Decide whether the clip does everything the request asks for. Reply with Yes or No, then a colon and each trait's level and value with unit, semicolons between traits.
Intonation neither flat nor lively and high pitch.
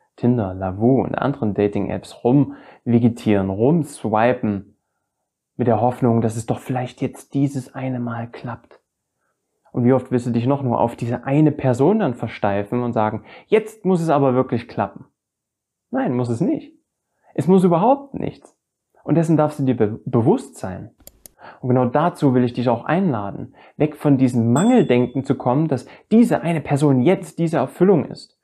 No: average, 4.0 semitones; low, 130 Hz